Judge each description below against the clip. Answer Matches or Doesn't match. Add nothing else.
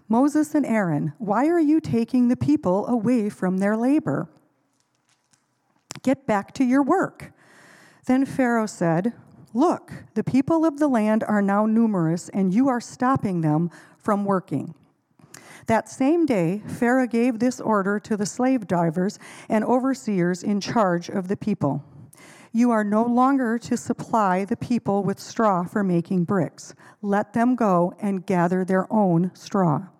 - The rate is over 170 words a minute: Doesn't match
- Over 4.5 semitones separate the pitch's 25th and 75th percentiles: Matches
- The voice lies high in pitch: Matches